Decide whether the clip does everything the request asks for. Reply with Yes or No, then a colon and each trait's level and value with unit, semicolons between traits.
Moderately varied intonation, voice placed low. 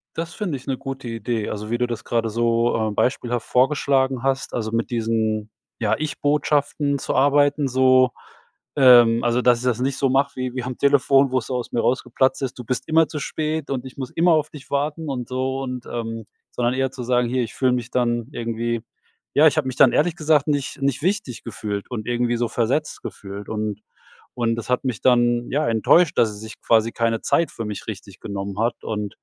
Yes: average, 3.0 semitones; low, 125 Hz